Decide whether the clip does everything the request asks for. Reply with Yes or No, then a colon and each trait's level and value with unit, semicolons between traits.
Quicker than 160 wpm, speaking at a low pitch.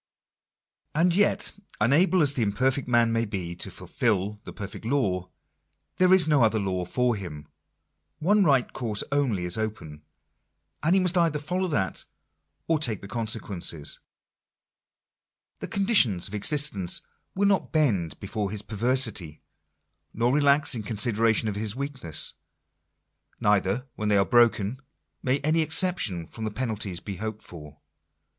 No: average, 145 wpm; low, 115 Hz